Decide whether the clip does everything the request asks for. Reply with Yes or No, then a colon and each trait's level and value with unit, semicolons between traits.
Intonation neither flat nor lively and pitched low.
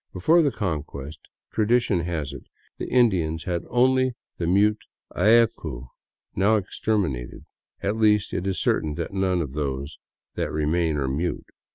No: wide, 5.9 semitones; very low, 90 Hz